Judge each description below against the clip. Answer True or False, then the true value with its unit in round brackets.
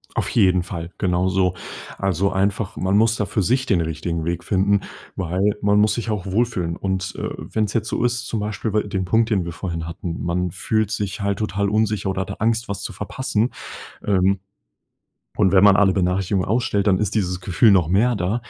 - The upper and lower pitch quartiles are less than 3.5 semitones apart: True (2.6 semitones)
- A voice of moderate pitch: False (100 Hz)